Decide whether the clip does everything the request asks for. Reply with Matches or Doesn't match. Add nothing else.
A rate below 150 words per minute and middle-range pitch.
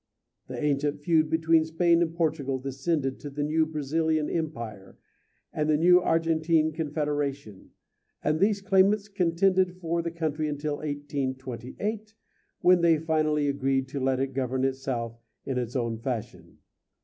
Matches